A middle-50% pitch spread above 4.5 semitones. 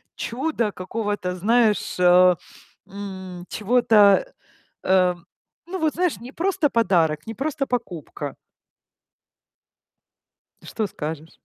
Yes: wide, 5.6 semitones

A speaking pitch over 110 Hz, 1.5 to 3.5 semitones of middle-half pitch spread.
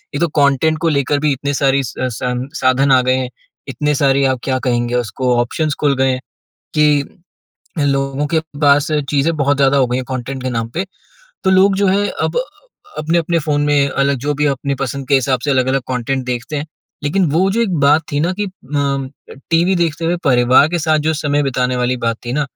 Yes: medium, 140 Hz; average, 2.7 semitones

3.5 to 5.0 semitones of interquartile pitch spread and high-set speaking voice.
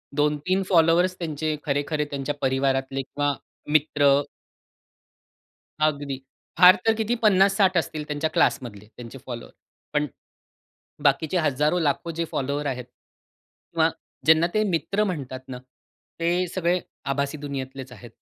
No: average, 3.9 semitones; medium, 150 Hz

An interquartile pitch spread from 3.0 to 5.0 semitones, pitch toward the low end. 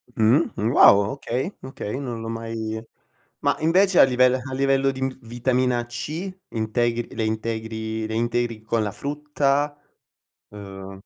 Yes: average, 3.5 semitones; low, 120 Hz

